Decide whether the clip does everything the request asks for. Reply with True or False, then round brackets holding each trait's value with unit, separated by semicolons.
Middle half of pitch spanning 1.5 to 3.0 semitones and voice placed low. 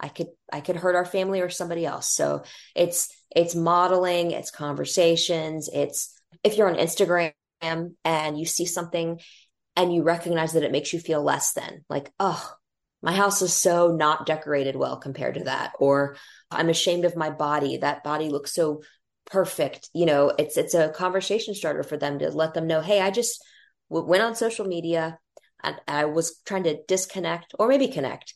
False (2.5 semitones; 170 Hz)